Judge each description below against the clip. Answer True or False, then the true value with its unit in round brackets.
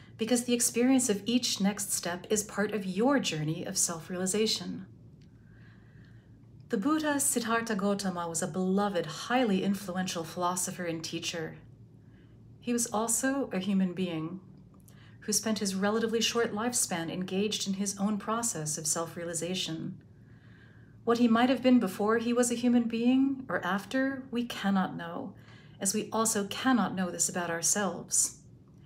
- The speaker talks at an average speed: True (145 wpm)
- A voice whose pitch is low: False (200 Hz)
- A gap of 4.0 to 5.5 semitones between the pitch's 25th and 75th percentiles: True (5.2 semitones)